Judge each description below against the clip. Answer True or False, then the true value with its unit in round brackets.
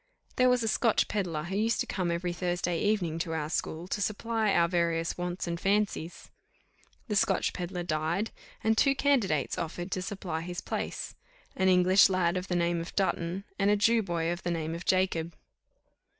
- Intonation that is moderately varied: True (3.1 semitones)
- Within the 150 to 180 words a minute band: False (190 wpm)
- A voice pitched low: False (180 Hz)